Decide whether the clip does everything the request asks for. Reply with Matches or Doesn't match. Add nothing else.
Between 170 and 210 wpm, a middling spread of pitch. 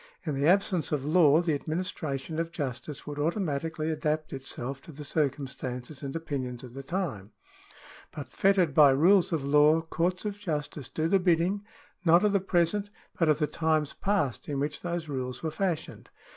Matches